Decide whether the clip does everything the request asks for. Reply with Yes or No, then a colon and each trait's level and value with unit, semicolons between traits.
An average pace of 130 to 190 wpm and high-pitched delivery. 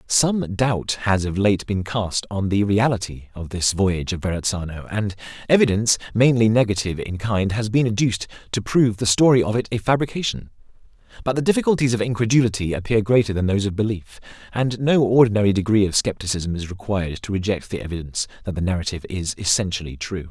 No: average, 180 wpm; low, 105 Hz